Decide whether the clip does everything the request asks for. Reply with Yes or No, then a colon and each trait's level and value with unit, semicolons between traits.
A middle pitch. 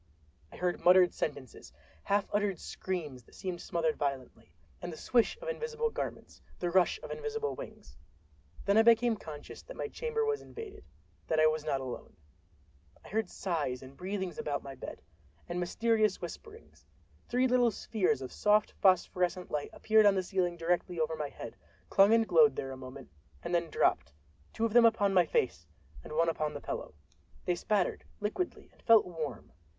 Yes: medium, 180 Hz